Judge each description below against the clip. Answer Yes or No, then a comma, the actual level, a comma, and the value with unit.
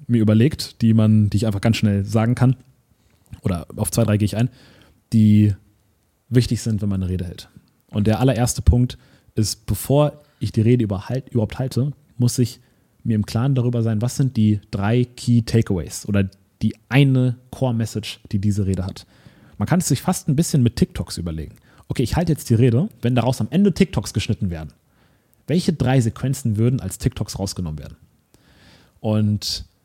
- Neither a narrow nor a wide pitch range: Yes, average, 3.4 semitones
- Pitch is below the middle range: Yes, low, 115 Hz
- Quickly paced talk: No, average, 180 wpm